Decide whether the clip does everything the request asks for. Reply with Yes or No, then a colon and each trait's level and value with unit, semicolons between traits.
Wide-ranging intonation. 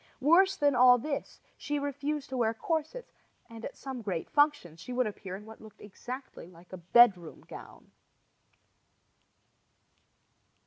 Yes: wide, 5.9 semitones